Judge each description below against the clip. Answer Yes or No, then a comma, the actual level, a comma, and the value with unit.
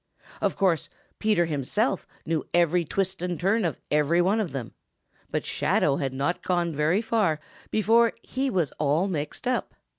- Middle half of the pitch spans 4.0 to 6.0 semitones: Yes, average, 5.2 semitones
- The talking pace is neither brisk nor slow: Yes, average, 160 wpm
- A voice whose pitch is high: No, medium, 175 Hz